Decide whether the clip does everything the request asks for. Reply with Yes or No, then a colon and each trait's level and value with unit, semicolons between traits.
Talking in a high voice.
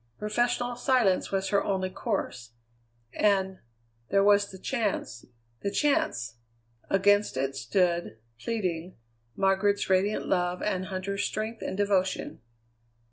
Yes: high, 195 Hz